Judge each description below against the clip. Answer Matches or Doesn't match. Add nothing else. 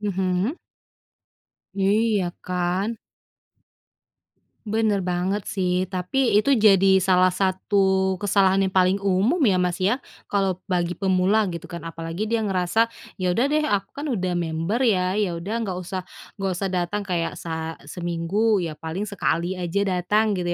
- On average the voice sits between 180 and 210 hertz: Matches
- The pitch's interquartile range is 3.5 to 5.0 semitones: Doesn't match